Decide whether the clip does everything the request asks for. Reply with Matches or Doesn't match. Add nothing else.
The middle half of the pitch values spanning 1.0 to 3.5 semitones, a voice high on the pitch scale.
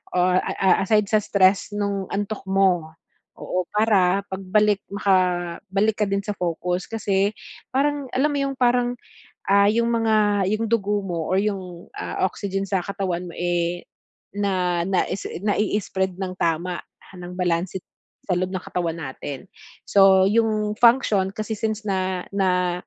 Matches